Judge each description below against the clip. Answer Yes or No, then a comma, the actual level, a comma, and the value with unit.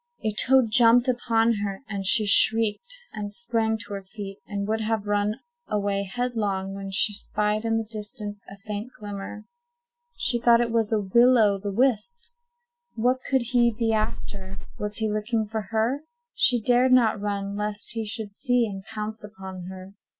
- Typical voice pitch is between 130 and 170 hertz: No, high, 215 Hz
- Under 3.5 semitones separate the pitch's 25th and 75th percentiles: Yes, narrow, 2.4 semitones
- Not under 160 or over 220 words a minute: Yes, average, 175 wpm